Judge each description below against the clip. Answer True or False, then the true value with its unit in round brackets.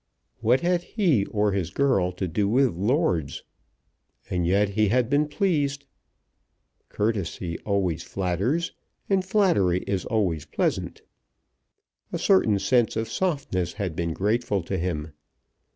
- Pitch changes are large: True (7.1 semitones)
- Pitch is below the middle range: True (105 Hz)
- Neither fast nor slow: False (130 wpm)